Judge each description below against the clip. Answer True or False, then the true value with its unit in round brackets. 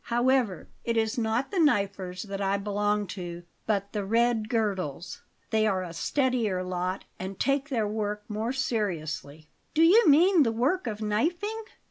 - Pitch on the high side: True (215 Hz)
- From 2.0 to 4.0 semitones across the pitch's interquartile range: False (4.6 semitones)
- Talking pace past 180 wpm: False (160 wpm)